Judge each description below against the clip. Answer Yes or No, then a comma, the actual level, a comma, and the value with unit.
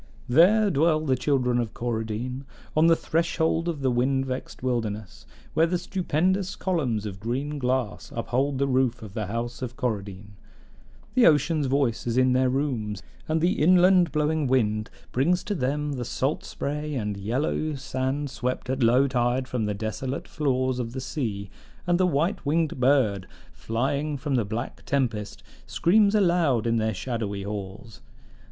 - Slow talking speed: No, average, 160 wpm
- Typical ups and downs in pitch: Yes, average, 4.7 semitones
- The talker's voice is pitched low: Yes, low, 130 Hz